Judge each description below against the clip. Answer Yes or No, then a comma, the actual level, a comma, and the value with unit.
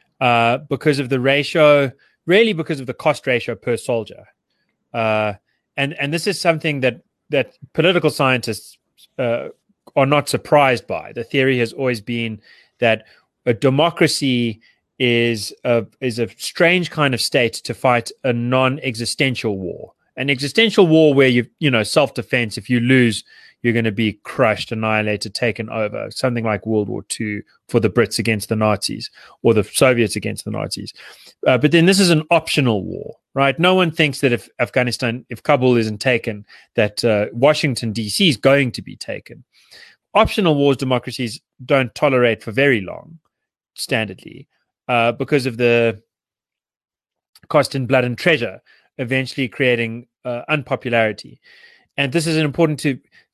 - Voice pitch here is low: Yes, low, 125 Hz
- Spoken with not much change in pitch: No, average, 3.7 semitones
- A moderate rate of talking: Yes, average, 160 wpm